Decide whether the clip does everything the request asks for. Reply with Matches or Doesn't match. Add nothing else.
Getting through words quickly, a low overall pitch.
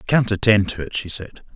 Matches